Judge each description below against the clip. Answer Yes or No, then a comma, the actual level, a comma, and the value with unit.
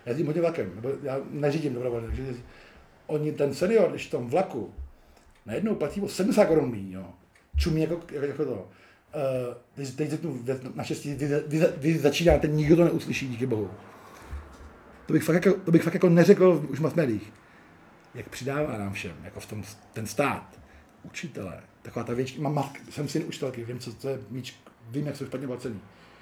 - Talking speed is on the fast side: Yes, fast, 175 wpm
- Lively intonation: Yes, wide, 5.8 semitones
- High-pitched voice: No, low, 135 Hz